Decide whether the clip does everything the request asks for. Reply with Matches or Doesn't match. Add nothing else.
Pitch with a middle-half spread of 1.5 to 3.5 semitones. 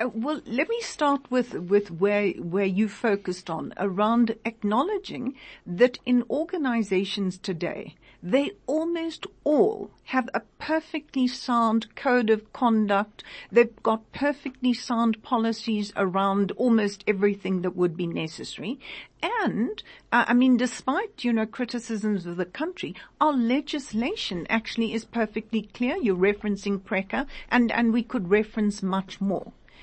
Doesn't match